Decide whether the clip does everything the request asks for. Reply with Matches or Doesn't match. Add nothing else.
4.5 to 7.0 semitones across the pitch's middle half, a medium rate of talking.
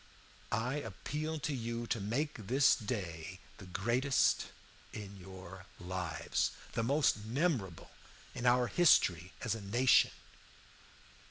Doesn't match